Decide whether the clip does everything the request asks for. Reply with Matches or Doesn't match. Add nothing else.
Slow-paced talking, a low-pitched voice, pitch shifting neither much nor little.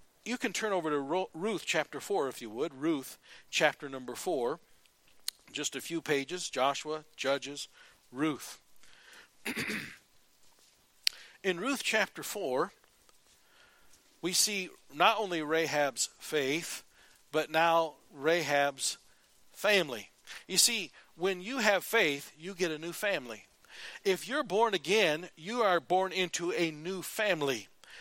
Doesn't match